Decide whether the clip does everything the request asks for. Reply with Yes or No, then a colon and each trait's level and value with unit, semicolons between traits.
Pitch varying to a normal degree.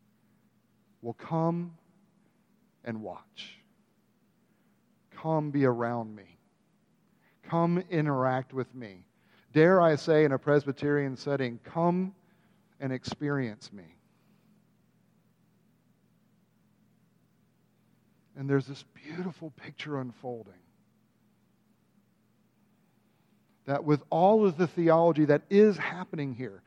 No: wide, 5.9 semitones